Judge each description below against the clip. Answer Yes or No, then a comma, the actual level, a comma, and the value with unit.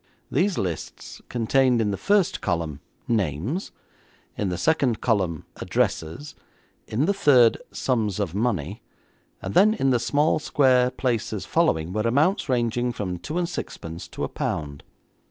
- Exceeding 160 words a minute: No, average, 145 wpm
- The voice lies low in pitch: Yes, low, 115 Hz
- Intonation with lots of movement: Yes, wide, 6.8 semitones